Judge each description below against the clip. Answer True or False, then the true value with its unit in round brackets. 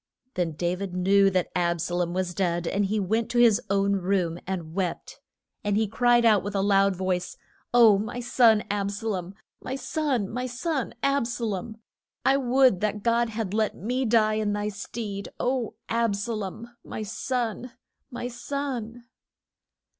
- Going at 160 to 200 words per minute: True (175 wpm)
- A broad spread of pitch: False (3.7 semitones)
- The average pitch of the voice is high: True (210 Hz)